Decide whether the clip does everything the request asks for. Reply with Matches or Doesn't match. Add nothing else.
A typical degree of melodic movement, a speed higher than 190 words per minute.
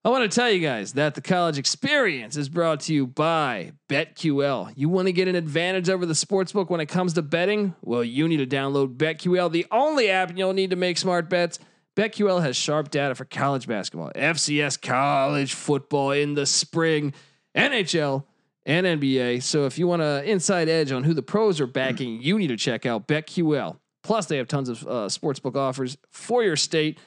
Matches